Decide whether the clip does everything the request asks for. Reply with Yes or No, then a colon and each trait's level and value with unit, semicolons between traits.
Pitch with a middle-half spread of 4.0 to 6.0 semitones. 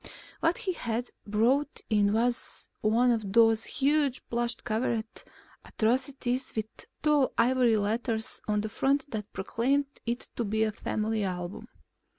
No: average, 3.1 semitones